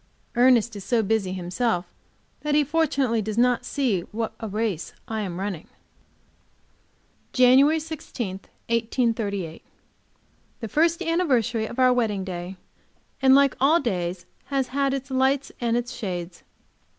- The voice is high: Yes, high, 235 Hz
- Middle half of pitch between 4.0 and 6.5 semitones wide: Yes, average, 5.2 semitones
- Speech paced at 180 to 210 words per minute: No, slow, 135 wpm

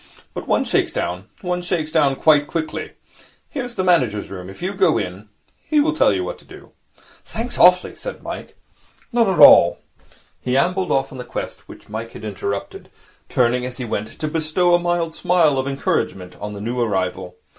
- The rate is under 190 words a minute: No, average, 195 wpm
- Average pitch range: No, wide, 8.7 semitones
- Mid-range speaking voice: Yes, medium, 145 Hz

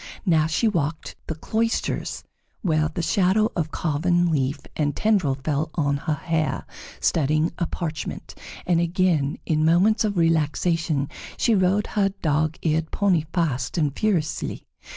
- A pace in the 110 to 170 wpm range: Yes, average, 140 wpm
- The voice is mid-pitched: Yes, medium, 165 Hz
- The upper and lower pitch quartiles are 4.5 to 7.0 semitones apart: No, average, 3.1 semitones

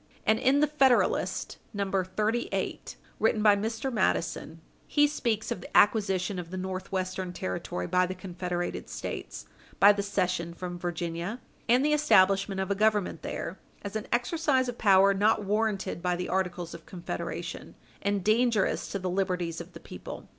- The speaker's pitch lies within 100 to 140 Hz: No, high, 195 Hz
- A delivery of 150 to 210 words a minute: Yes, average, 160 wpm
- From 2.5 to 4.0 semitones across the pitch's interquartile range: Yes, average, 3.3 semitones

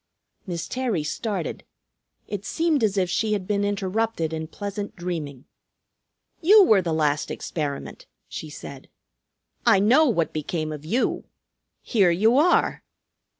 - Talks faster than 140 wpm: No, slow, 135 wpm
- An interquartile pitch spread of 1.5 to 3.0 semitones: No, wide, 5.6 semitones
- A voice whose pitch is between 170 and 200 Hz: Yes, high, 190 Hz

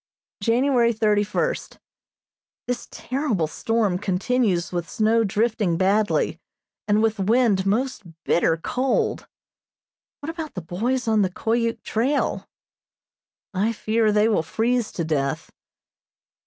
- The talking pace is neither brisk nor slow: No, slow, 115 wpm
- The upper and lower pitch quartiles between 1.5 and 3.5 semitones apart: No, average, 3.9 semitones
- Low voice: No, high, 220 Hz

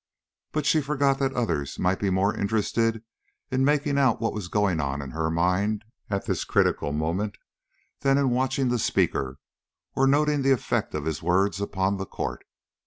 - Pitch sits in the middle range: No, low, 105 Hz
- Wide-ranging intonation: Yes, wide, 6.9 semitones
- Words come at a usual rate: Yes, average, 175 wpm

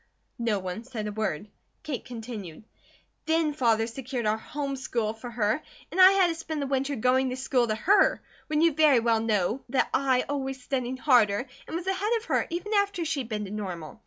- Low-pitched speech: No, very high, 255 Hz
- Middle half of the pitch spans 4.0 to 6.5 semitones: Yes, wide, 5.6 semitones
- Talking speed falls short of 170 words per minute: No, fast, 205 wpm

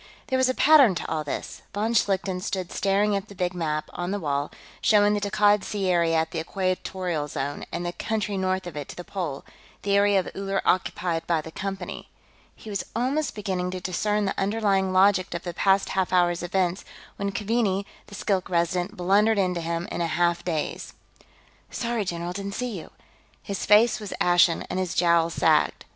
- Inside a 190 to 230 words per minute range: Yes, average, 195 wpm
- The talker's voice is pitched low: No, high, 190 Hz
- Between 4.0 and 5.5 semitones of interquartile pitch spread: No, average, 2.8 semitones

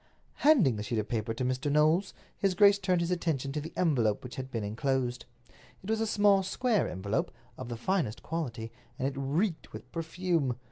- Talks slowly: No, average, 195 wpm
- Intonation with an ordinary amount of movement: No, wide, 7.1 semitones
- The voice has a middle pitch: Yes, medium, 145 Hz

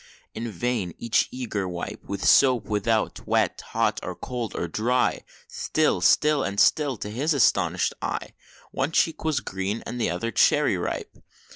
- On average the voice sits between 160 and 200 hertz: No, low, 115 Hz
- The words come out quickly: No, average, 155 wpm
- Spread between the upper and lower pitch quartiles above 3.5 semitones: Yes, average, 4.2 semitones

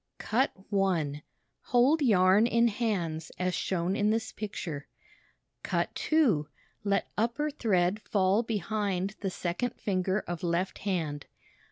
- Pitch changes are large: No, average, 3.9 semitones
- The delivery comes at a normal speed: No, slow, 125 wpm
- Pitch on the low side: No, high, 195 Hz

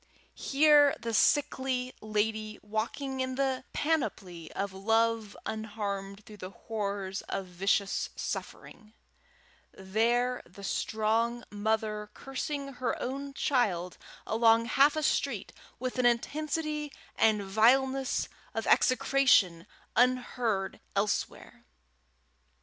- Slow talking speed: Yes, slow, 100 wpm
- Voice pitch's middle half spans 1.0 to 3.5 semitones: No, average, 4.3 semitones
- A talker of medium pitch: No, high, 225 Hz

